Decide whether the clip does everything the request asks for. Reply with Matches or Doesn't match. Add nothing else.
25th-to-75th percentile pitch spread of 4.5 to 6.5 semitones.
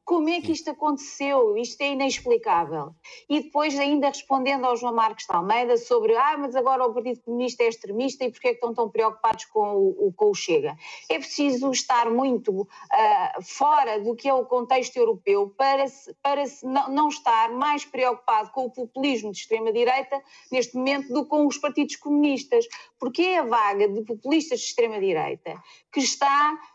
Doesn't match